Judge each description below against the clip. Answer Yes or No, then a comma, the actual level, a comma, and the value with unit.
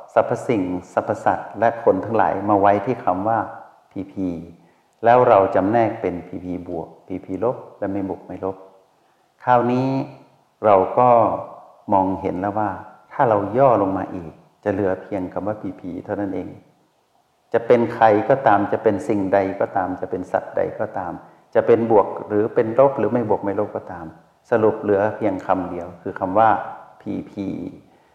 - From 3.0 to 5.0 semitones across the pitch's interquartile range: No, narrow, 2.6 semitones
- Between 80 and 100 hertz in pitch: Yes, very low, 95 Hz